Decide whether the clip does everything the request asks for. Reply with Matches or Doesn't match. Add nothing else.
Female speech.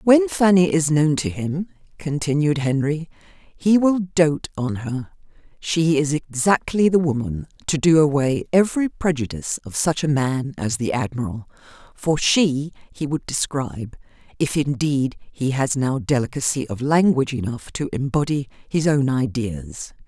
Matches